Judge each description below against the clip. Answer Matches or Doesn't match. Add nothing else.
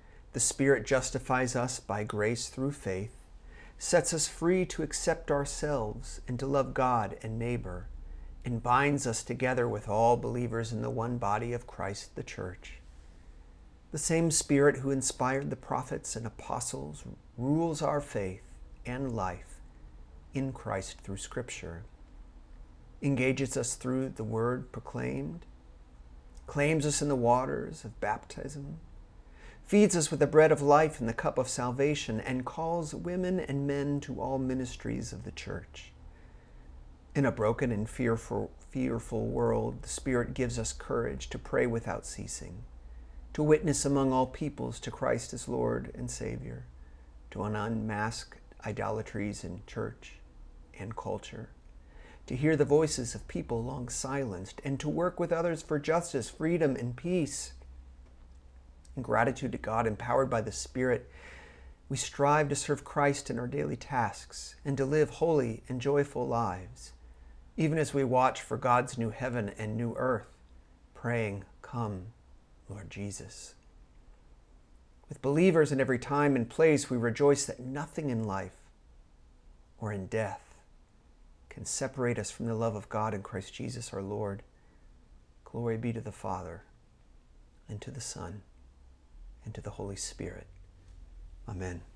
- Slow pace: Doesn't match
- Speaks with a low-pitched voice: Matches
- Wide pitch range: Matches